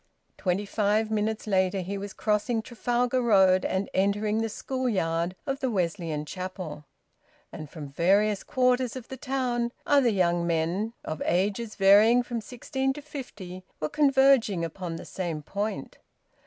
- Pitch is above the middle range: Yes, high, 205 Hz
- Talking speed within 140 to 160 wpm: Yes, average, 150 wpm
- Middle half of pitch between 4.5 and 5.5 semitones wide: Yes, average, 4.9 semitones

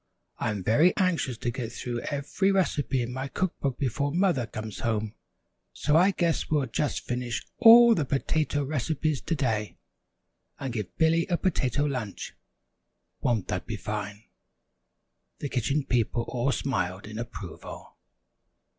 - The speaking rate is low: No, average, 145 wpm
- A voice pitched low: Yes, low, 130 Hz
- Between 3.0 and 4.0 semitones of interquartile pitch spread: No, wide, 5.5 semitones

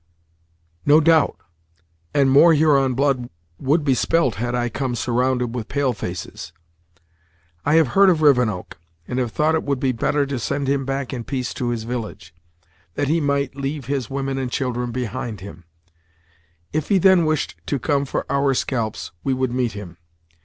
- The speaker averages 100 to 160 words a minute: No, average, 175 wpm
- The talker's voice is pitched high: No, low, 135 Hz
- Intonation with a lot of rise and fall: No, average, 2.8 semitones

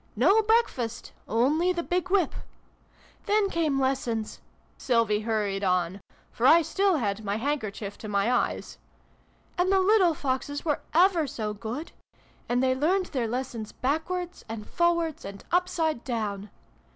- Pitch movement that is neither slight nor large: No, wide, 7.8 semitones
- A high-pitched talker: Yes, very high, 265 Hz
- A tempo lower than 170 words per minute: Yes, average, 145 wpm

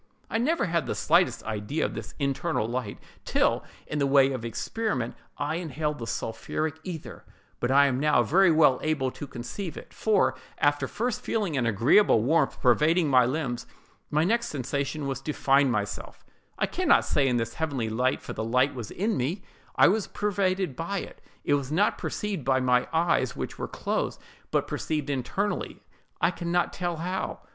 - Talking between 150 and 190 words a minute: Yes, average, 185 wpm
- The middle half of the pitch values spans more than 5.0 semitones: Yes, wide, 5.4 semitones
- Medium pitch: Yes, medium, 145 Hz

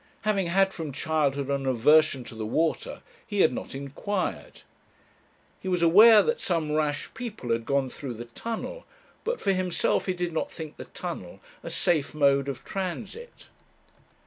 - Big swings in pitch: Yes, wide, 5.7 semitones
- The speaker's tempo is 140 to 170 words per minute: Yes, average, 165 wpm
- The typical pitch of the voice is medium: Yes, medium, 160 Hz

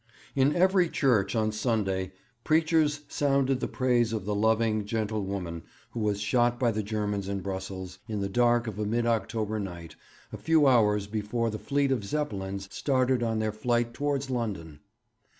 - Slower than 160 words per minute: No, average, 170 wpm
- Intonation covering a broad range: No, average, 3.9 semitones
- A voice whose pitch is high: No, low, 110 Hz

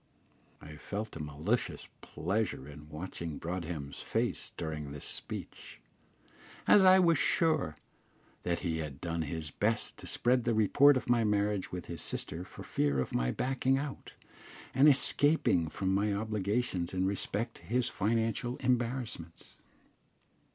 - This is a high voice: No, low, 100 Hz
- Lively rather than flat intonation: Yes, wide, 7.1 semitones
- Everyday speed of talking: Yes, average, 145 wpm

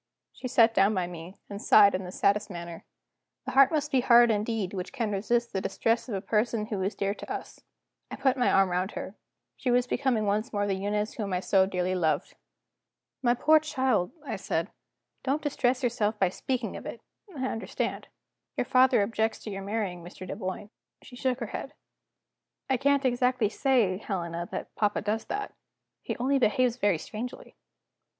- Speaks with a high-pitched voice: Yes, high, 215 Hz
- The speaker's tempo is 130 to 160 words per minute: No, average, 185 wpm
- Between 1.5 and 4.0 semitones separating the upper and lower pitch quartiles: No, average, 4.4 semitones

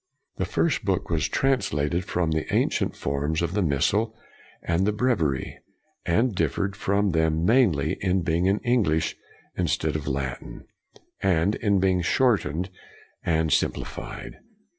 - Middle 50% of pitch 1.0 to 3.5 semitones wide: No, average, 4.4 semitones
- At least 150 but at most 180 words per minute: No, average, 140 wpm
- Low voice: Yes, very low, 90 Hz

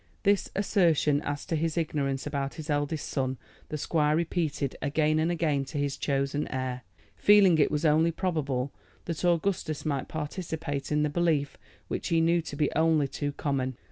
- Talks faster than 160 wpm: Yes, average, 170 wpm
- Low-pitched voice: No, medium, 150 Hz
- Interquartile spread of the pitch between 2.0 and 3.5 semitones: Yes, narrow, 2.6 semitones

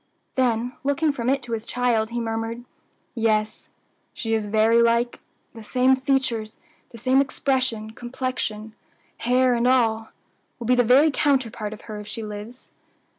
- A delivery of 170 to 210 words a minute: No, average, 155 wpm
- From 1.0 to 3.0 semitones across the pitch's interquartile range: Yes, narrow, 2.6 semitones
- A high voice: Yes, high, 235 Hz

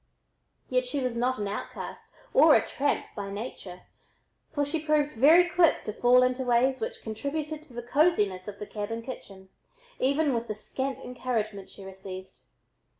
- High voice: Yes, very high, 250 Hz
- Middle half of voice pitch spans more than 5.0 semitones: Yes, wide, 5.4 semitones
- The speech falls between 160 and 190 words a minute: Yes, average, 165 wpm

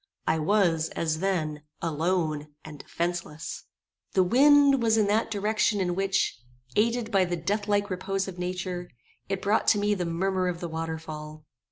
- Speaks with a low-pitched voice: No, medium, 185 Hz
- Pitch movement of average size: Yes, average, 3.9 semitones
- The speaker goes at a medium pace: Yes, average, 165 wpm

